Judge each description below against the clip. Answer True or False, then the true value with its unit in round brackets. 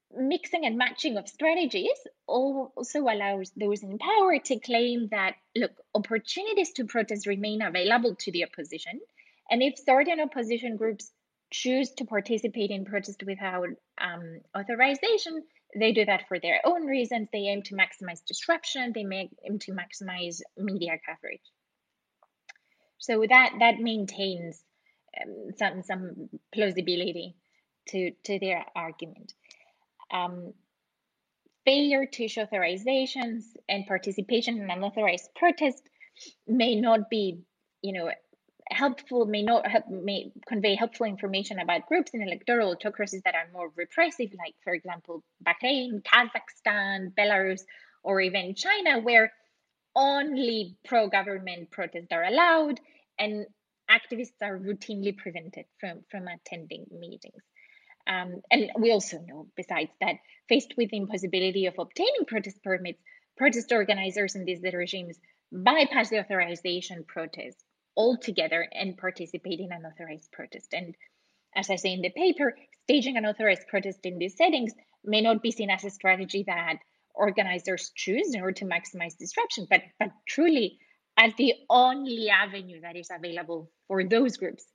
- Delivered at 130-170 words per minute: True (140 wpm)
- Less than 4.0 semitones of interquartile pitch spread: False (4.9 semitones)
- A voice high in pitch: True (210 Hz)